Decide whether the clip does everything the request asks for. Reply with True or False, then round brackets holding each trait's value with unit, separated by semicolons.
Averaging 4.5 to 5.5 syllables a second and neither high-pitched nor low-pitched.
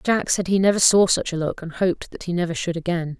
False (6.4 syllables/s; 175 Hz)